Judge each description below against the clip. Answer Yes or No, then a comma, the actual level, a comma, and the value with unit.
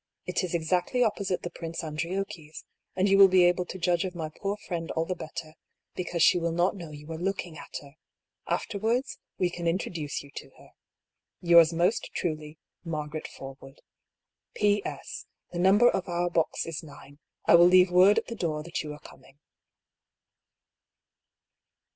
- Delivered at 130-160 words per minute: No, average, 190 wpm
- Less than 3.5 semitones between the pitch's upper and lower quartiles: Yes, average, 2.8 semitones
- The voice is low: No, medium, 175 Hz